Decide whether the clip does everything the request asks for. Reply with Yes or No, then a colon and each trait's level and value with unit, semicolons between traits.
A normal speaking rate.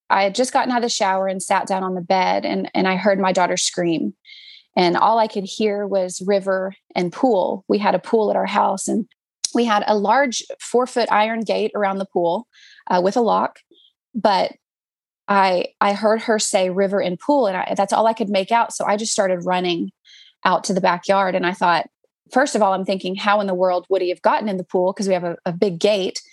No: fast, 240 wpm